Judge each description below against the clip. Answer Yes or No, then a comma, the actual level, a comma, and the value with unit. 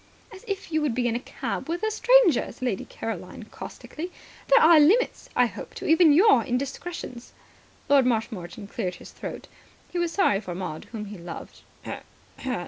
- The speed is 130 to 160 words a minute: No, average, 175 wpm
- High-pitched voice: Yes, very high, 265 Hz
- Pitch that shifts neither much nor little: No, wide, 8.0 semitones